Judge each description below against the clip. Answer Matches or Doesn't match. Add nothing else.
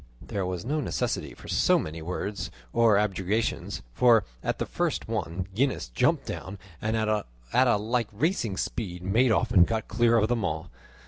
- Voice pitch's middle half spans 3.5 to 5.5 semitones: Matches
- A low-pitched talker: Matches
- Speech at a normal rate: Matches